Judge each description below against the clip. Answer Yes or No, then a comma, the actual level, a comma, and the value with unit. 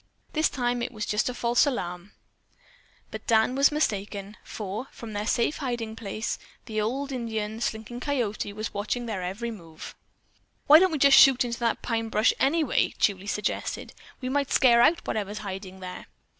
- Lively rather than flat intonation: No, average, 3.4 semitones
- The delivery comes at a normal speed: Yes, average, 170 wpm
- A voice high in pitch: Yes, high, 225 Hz